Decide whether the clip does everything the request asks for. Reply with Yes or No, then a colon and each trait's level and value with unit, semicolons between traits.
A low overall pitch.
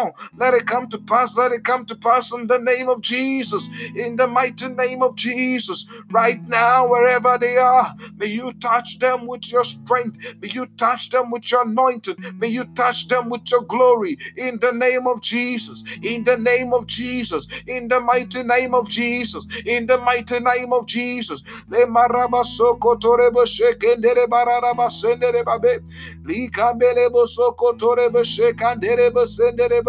No: high, 245 Hz